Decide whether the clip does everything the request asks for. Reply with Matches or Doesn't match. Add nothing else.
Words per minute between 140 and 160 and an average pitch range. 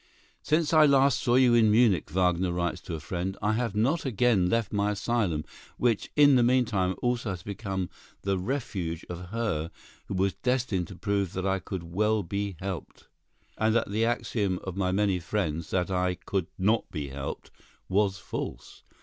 Doesn't match